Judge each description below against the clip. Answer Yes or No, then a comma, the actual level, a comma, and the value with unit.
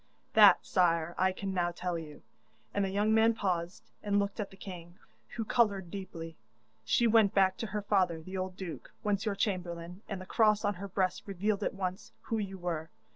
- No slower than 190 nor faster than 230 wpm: Yes, average, 200 wpm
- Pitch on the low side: No, high, 190 Hz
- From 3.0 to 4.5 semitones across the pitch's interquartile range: No, narrow, 2.6 semitones